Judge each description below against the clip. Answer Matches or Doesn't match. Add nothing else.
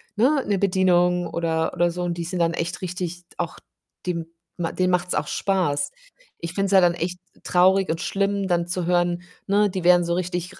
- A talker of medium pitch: Matches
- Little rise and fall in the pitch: Matches